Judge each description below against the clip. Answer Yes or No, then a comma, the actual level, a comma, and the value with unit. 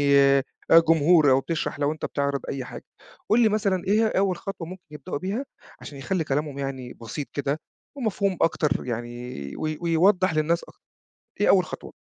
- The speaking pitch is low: No, medium, 155 Hz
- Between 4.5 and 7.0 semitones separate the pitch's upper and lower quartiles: Yes, average, 5.1 semitones